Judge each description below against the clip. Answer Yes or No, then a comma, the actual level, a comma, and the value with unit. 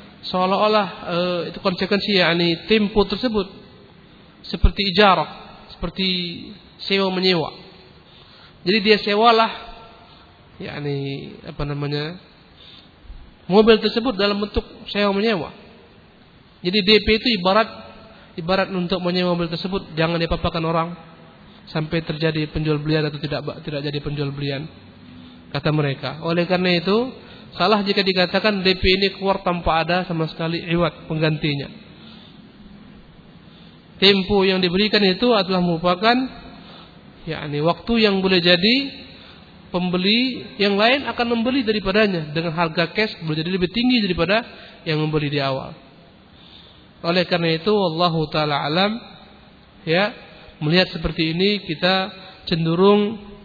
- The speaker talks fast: No, average, 120 wpm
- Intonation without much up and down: No, average, 4.0 semitones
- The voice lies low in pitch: No, medium, 185 Hz